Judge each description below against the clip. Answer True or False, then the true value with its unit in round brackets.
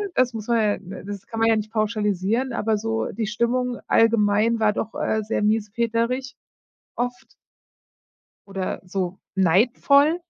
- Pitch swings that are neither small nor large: False (2.2 semitones)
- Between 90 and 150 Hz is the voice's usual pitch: False (220 Hz)